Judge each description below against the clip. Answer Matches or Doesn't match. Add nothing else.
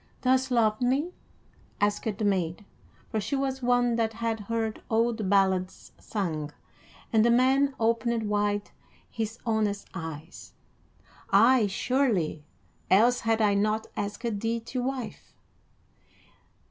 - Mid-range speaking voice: Doesn't match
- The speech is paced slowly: Matches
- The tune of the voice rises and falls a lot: Doesn't match